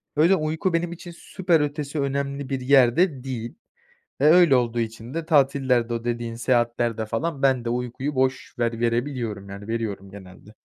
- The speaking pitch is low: Yes, low, 130 Hz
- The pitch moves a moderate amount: Yes, average, 3.9 semitones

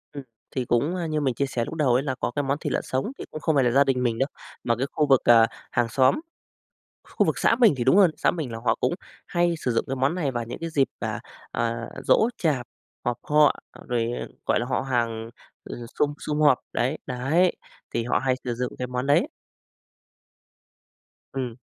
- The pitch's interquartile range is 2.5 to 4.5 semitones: Yes, average, 3.6 semitones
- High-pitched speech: No, low, 130 Hz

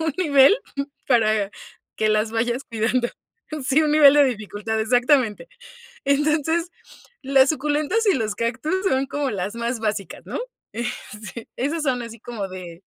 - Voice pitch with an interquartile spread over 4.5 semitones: Yes, average, 4.9 semitones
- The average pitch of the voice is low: No, high, 245 Hz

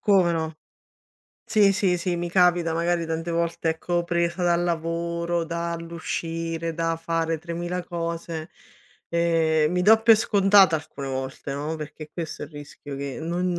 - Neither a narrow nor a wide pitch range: No, narrow, 1.3 semitones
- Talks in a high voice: No, medium, 170 Hz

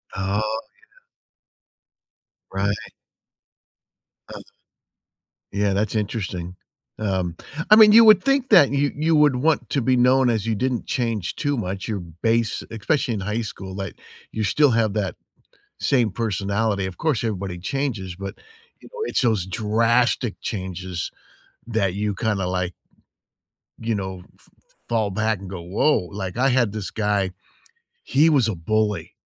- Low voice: Yes, low, 110 Hz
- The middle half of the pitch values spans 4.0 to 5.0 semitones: Yes, average, 4.4 semitones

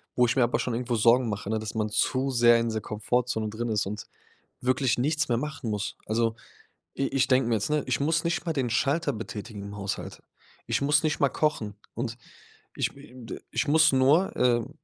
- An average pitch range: Yes, average, 3.9 semitones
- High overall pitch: No, low, 120 Hz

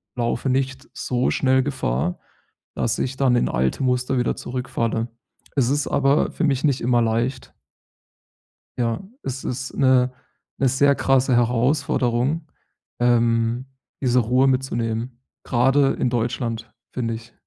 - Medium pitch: No, low, 125 Hz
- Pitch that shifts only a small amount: Yes, narrow, 2.0 semitones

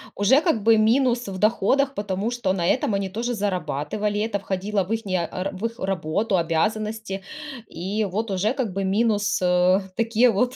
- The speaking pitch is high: Yes, high, 205 Hz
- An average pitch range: Yes, average, 3.1 semitones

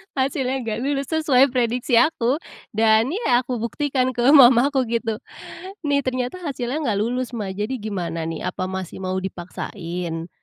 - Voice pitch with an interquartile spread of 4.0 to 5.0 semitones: Yes, average, 4.6 semitones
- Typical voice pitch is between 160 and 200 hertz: No, high, 240 Hz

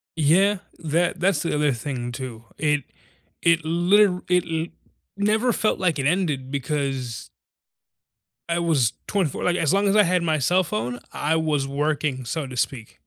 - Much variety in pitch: No, average, 4.7 semitones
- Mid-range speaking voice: Yes, medium, 155 Hz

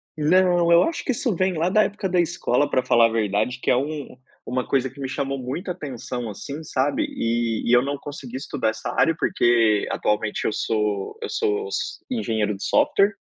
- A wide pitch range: Yes, wide, 6.9 semitones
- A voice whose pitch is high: No, low, 135 Hz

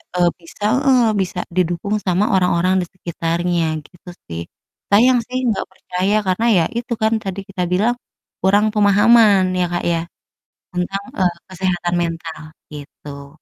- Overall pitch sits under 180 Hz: No, medium, 185 Hz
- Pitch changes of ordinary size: Yes, average, 3.0 semitones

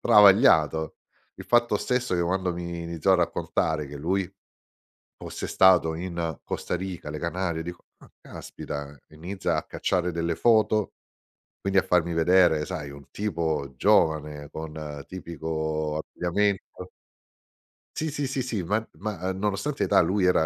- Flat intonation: No, average, 3.6 semitones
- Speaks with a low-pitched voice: Yes, very low, 85 Hz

